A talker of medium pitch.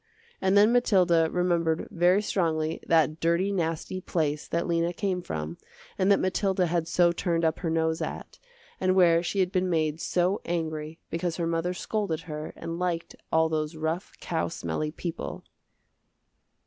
Yes: medium, 170 Hz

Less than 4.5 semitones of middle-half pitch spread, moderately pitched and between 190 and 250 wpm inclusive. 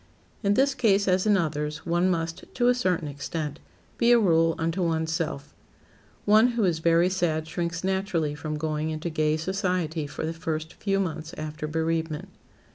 No: average, 3.3 semitones; medium, 165 Hz; average, 175 wpm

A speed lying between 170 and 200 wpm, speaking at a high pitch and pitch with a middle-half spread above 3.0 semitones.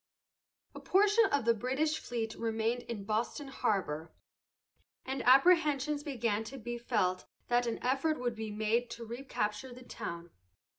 No: average, 145 wpm; high, 240 Hz; average, 3.7 semitones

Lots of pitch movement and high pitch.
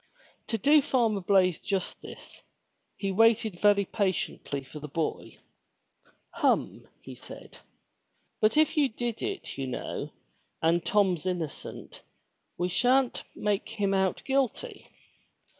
No: average, 4.8 semitones; high, 200 Hz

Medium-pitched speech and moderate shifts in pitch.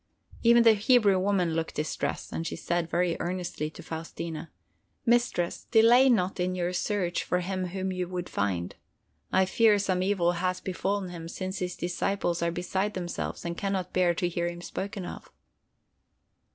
No: medium, 180 Hz; narrow, 2.3 semitones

